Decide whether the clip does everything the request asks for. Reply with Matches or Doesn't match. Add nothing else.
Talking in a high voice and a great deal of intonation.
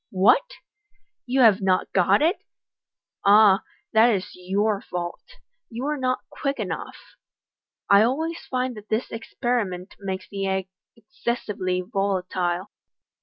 Doesn't match